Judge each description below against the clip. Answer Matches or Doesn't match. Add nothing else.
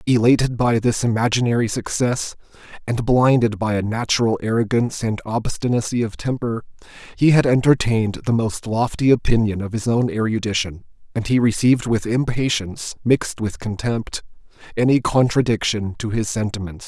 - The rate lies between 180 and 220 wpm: Doesn't match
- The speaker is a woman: Doesn't match